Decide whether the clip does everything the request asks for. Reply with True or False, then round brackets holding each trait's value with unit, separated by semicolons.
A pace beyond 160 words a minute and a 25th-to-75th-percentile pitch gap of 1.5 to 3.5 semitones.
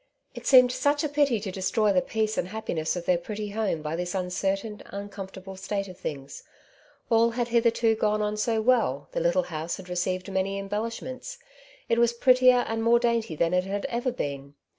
False (190 wpm; 4.3 semitones)